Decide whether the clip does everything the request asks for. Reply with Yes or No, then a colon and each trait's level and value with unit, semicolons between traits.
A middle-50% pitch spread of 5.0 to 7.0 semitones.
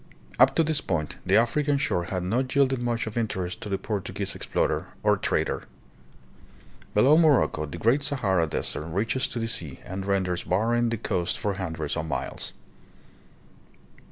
Yes: average, 5.3 semitones